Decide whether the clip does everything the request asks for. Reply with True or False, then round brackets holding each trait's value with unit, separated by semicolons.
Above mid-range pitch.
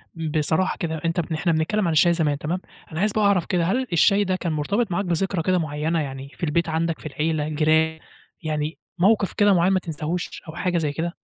False (165 Hz)